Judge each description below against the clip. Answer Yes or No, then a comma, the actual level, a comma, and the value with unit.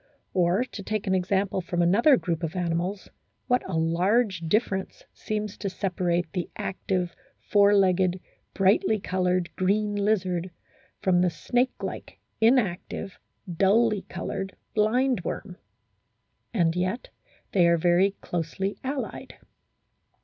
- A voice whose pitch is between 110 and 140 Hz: No, high, 190 Hz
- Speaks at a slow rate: Yes, slow, 120 wpm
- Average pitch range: Yes, average, 3.0 semitones